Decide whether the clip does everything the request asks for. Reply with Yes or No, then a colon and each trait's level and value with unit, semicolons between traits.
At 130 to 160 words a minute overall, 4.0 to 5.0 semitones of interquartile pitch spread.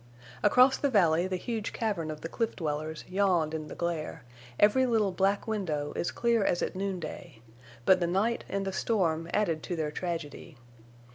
No: average, 180 wpm; average, 4.5 semitones